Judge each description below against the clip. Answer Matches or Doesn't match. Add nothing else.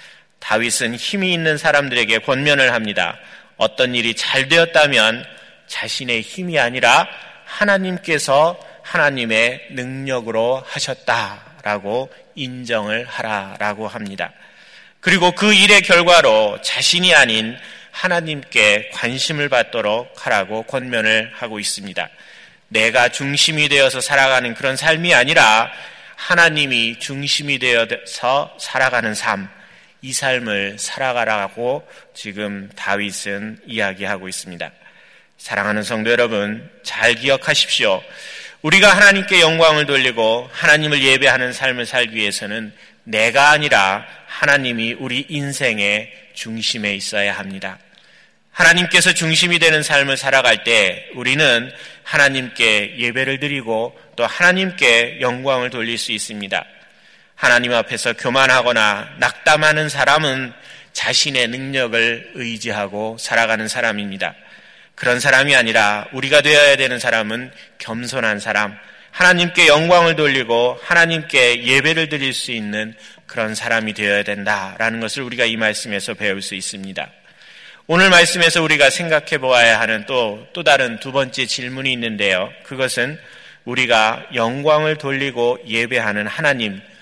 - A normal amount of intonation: Matches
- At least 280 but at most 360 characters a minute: Matches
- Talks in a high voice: Doesn't match